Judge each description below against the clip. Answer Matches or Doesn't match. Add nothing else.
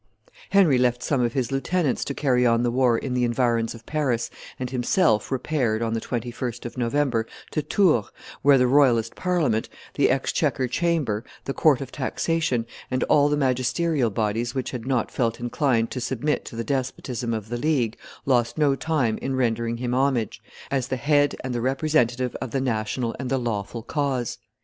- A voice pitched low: Matches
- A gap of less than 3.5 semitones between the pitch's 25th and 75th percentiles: Matches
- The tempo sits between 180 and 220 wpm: Matches